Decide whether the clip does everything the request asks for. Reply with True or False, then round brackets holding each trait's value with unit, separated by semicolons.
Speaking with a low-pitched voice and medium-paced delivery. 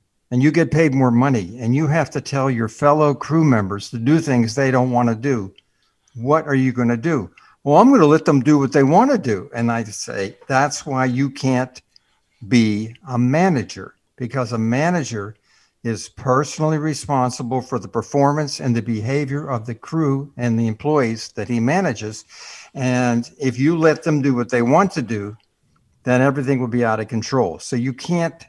True (130 Hz; 195 wpm)